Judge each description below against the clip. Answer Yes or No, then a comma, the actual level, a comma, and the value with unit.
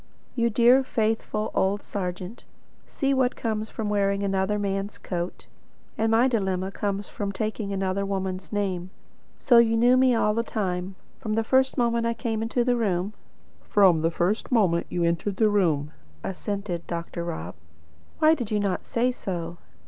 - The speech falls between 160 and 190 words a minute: Yes, average, 165 wpm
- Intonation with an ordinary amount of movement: Yes, average, 3.6 semitones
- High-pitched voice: Yes, high, 205 Hz